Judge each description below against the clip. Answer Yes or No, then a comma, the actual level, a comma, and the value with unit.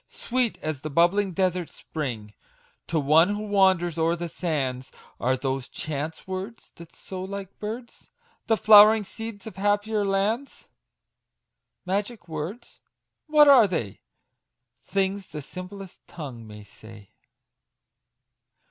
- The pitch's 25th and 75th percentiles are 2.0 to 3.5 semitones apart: No, average, 5.1 semitones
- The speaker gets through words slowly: Yes, slow, 120 wpm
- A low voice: No, medium, 185 Hz